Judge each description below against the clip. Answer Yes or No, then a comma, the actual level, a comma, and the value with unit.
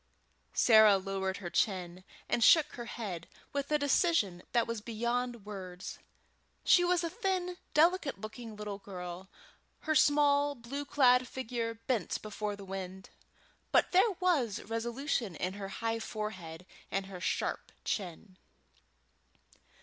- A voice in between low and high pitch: No, high, 225 Hz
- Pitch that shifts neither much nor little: No, wide, 6.4 semitones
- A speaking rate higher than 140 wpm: No, slow, 135 wpm